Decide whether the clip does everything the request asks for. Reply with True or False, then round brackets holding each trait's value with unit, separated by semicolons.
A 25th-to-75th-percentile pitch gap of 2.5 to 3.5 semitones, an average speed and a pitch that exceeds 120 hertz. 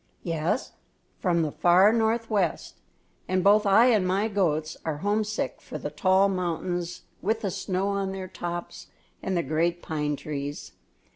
True (3.1 semitones; 150 wpm; 185 Hz)